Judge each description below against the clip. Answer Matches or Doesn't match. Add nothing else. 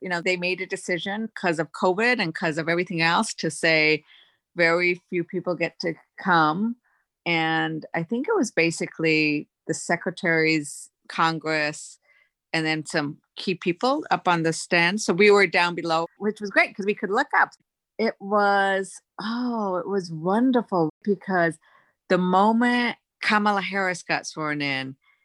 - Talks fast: Doesn't match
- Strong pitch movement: Doesn't match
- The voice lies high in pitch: Doesn't match